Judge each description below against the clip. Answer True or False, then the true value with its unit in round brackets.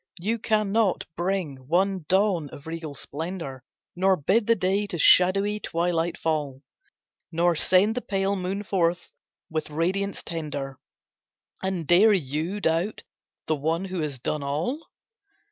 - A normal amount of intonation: True (3.9 semitones)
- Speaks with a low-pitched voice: False (175 Hz)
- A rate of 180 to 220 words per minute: False (135 wpm)